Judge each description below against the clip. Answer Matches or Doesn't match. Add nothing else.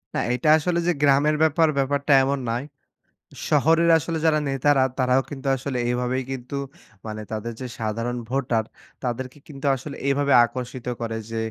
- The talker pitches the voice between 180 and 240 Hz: Doesn't match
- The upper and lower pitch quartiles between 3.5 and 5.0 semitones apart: Doesn't match